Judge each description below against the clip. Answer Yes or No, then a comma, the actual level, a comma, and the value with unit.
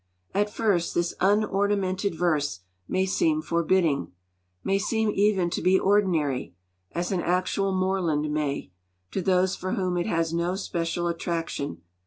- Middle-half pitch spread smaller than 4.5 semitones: Yes, average, 2.7 semitones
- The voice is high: No, medium, 180 Hz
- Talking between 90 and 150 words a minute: Yes, average, 140 wpm